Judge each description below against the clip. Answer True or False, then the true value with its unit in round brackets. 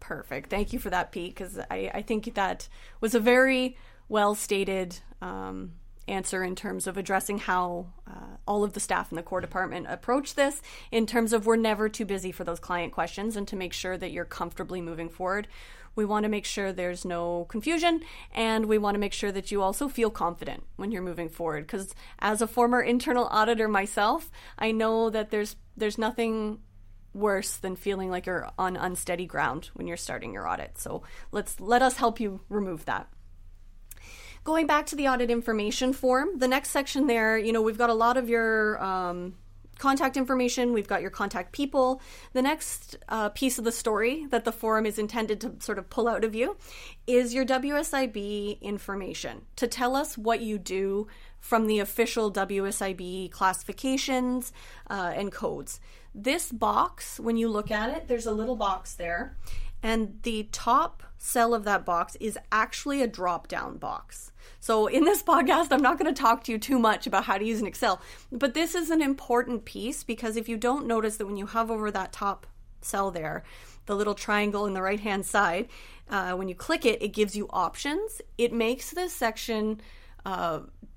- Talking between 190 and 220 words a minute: True (195 wpm)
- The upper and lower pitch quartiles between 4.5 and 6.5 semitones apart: False (4.1 semitones)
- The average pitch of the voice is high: True (215 Hz)